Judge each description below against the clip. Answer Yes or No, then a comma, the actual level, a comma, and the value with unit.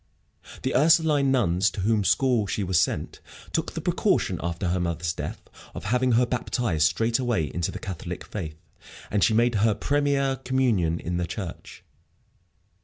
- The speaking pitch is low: Yes, low, 110 Hz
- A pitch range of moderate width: No, wide, 6.6 semitones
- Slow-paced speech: No, average, 160 wpm